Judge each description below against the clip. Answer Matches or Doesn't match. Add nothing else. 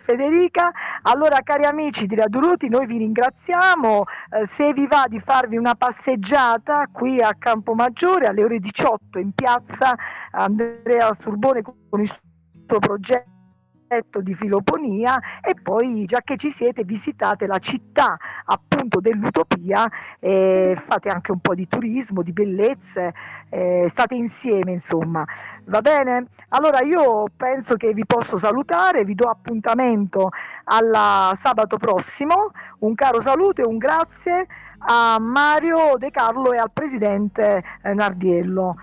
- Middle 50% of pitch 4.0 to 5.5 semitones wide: Matches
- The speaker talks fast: Doesn't match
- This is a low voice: Doesn't match